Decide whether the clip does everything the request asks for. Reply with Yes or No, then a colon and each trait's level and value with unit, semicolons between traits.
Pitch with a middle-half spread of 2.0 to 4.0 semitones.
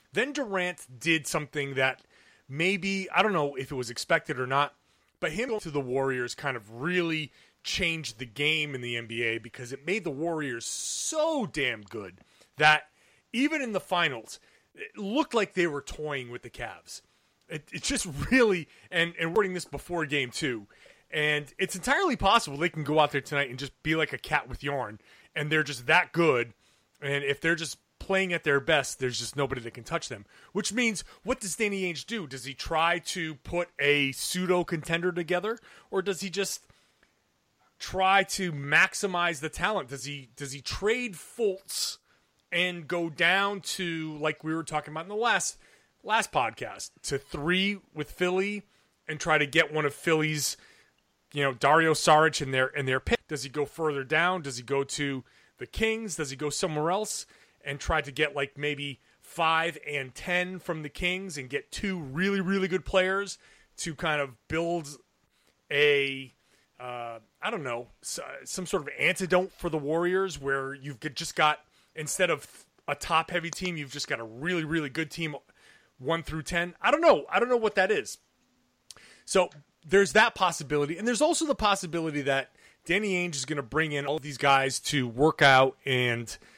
No: average, 4.8 semitones